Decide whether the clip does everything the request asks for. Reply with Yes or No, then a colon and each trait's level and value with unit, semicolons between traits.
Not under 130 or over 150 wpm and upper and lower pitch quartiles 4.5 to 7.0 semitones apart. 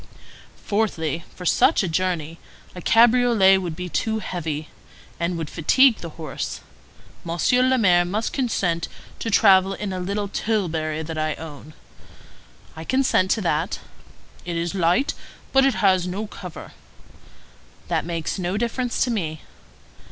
Yes: average, 145 wpm; average, 4.8 semitones